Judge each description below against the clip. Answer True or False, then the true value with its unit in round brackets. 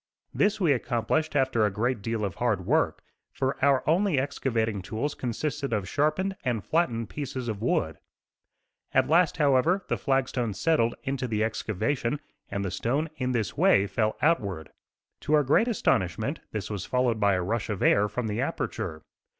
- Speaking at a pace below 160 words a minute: False (175 wpm)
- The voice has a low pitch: True (125 Hz)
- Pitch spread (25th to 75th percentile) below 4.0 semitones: False (5.3 semitones)